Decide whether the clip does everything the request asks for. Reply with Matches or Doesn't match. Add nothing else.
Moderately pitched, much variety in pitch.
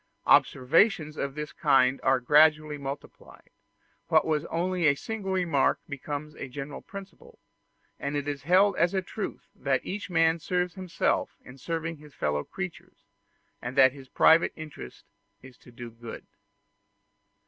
Doesn't match